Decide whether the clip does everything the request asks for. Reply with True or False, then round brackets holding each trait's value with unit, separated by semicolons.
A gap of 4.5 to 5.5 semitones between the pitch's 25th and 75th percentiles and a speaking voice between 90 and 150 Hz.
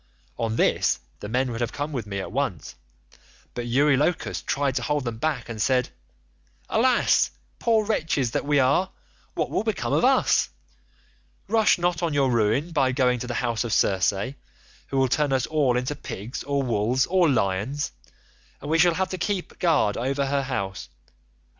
False (4.1 semitones; 135 Hz)